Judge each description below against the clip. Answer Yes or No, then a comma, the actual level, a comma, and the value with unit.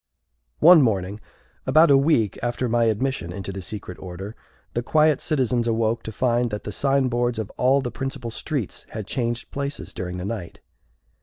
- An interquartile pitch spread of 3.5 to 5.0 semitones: Yes, average, 4.3 semitones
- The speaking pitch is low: Yes, low, 120 Hz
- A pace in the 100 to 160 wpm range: No, average, 170 wpm